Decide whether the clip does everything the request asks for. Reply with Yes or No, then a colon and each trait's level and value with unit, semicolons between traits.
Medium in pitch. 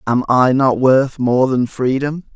No: low, 130 Hz